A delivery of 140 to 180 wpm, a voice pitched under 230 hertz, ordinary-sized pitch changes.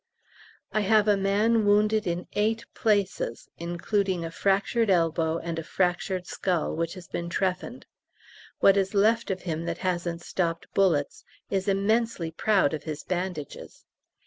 Yes: average, 145 wpm; medium, 185 Hz; average, 3.4 semitones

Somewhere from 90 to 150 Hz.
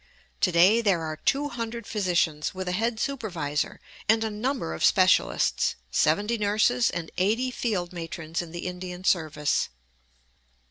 No: medium, 185 Hz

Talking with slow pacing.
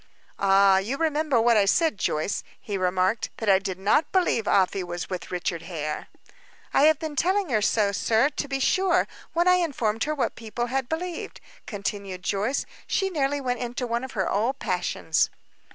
No: average, 185 wpm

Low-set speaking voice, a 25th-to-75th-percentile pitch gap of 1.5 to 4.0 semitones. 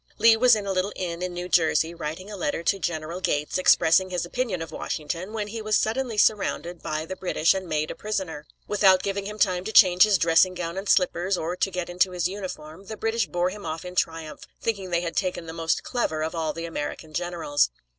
No: medium, 180 Hz; average, 3.4 semitones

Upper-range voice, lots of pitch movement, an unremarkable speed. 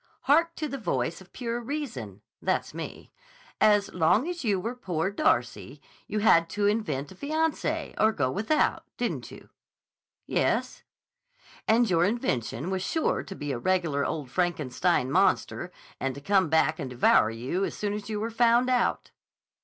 Yes: high, 195 Hz; wide, 7.7 semitones; average, 165 wpm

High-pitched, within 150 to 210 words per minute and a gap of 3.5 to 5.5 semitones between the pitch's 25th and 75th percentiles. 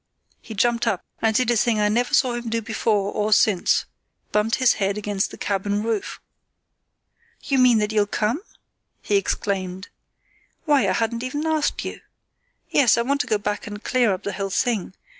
No: high, 220 Hz; average, 180 wpm; average, 2.8 semitones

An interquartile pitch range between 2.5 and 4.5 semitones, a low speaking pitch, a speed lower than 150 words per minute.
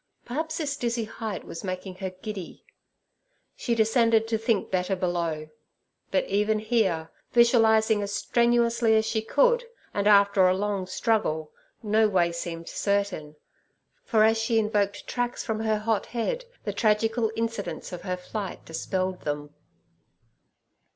No: average, 3.5 semitones; high, 215 Hz; average, 140 wpm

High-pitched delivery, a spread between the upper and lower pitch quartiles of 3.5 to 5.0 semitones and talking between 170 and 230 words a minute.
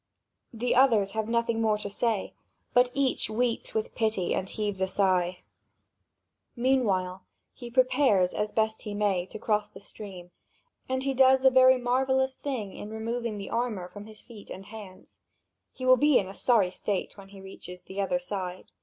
Yes: high, 215 Hz; average, 4.2 semitones; average, 180 wpm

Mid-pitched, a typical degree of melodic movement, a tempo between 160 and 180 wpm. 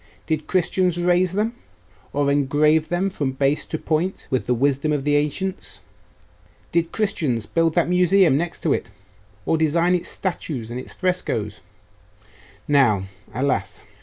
No: medium, 155 Hz; average, 4.4 semitones; average, 145 wpm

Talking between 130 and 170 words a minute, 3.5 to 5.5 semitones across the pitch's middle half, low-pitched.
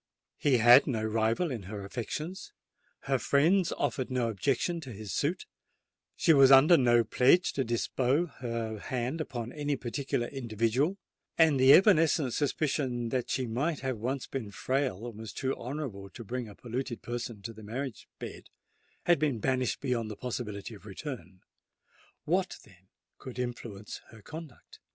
Yes: average, 150 wpm; average, 3.8 semitones; low, 125 Hz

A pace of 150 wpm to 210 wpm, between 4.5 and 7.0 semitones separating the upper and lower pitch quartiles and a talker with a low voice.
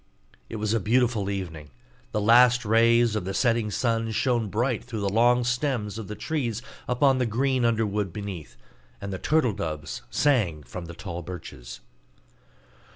No: average, 160 wpm; average, 4.0 semitones; low, 110 Hz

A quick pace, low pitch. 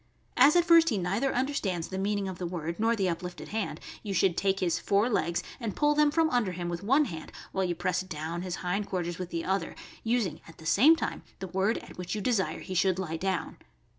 No: fast, 240 wpm; high, 190 Hz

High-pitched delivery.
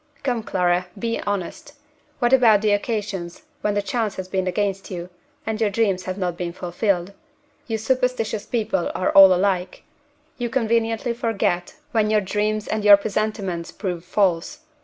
Yes: high, 205 Hz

